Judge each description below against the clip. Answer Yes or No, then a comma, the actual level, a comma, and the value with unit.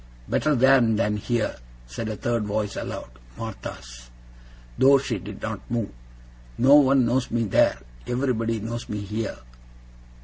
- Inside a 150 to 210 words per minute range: No, average, 140 wpm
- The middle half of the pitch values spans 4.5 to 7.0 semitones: No, average, 3.0 semitones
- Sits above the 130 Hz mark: No, low, 115 Hz